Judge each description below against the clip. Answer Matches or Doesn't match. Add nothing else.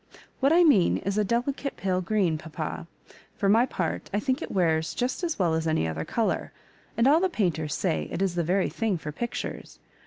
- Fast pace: Matches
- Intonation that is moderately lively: Doesn't match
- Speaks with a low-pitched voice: Doesn't match